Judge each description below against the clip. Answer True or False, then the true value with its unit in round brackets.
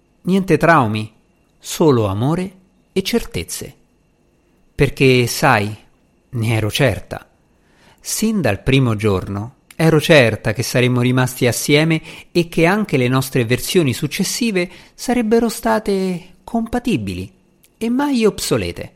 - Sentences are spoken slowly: True (110 wpm)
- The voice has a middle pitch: True (150 Hz)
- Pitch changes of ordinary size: False (7.6 semitones)